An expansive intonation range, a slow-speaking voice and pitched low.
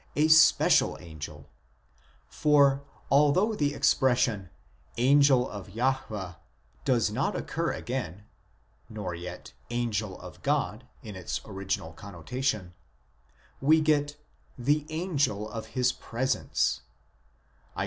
Yes: wide, 6.2 semitones; slow, 115 wpm; low, 125 Hz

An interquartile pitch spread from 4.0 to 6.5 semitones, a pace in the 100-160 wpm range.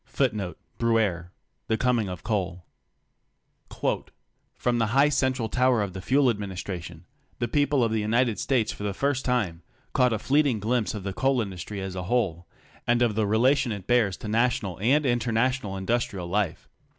Yes: average, 4.4 semitones; average, 155 wpm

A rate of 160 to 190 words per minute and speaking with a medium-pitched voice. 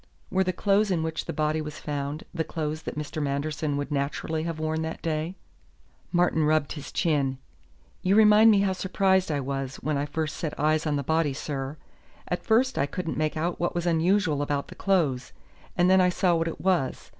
No: fast, 205 wpm; medium, 160 Hz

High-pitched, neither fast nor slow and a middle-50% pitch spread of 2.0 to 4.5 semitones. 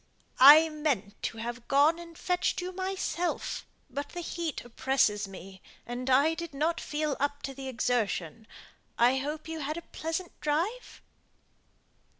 No: very high, 290 Hz; average, 150 wpm; average, 4.9 semitones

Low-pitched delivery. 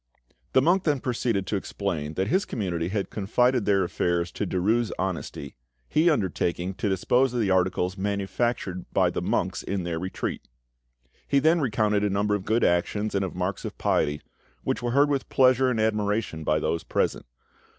Yes: low, 100 Hz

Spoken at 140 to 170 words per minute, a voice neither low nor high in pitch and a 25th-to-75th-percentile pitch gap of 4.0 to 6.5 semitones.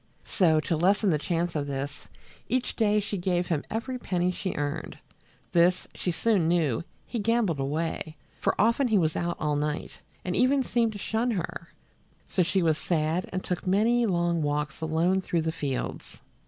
No: average, 180 wpm; medium, 175 Hz; average, 4.6 semitones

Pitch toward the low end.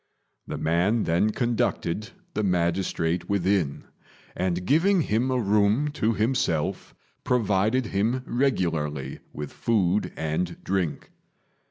Yes: low, 100 Hz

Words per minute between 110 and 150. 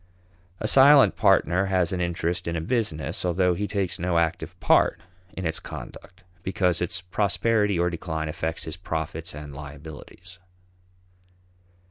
Yes: average, 140 wpm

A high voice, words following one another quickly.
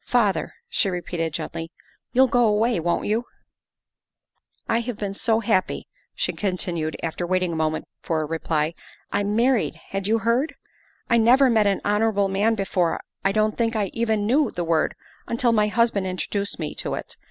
No: high, 205 Hz; average, 185 wpm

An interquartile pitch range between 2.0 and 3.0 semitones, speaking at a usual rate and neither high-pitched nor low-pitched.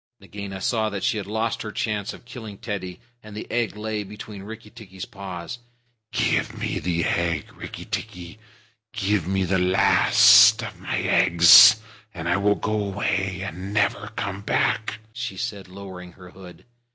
No: narrow, 2.6 semitones; average, 165 wpm; low, 100 Hz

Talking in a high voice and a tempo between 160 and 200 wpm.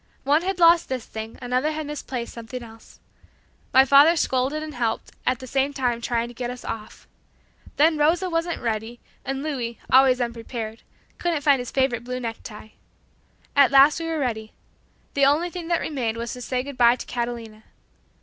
Yes: very high, 255 Hz; average, 180 wpm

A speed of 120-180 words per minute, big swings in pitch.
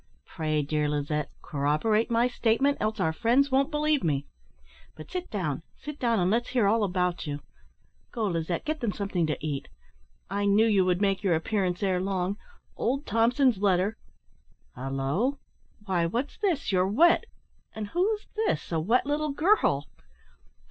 Yes: average, 160 wpm; wide, 7.0 semitones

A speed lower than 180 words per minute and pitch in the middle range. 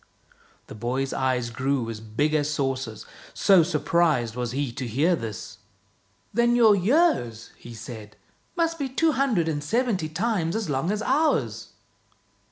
Yes: average, 160 wpm; medium, 150 Hz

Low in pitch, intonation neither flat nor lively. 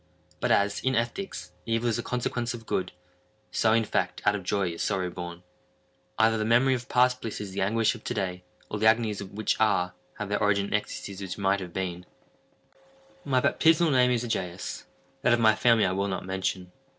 Yes: low, 105 Hz; average, 3.8 semitones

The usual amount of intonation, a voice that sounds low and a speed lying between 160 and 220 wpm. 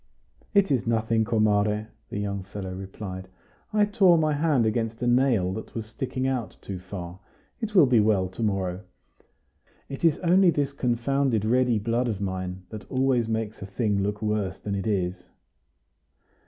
Yes: average, 4.6 semitones; low, 110 Hz; average, 170 wpm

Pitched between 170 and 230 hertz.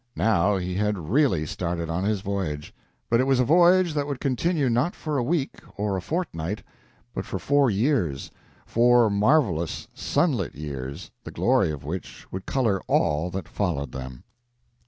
No: low, 105 Hz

